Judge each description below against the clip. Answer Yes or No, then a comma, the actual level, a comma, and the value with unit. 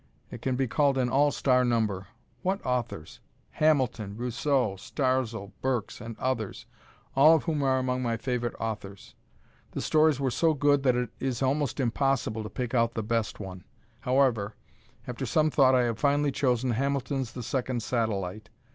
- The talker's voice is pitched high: No, low, 125 Hz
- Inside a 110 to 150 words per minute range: No, average, 165 wpm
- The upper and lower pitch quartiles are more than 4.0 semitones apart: No, average, 3.2 semitones